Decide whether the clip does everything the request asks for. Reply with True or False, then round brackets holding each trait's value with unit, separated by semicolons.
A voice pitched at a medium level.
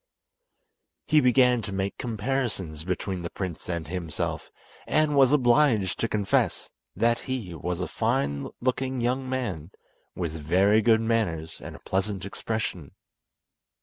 False (105 Hz)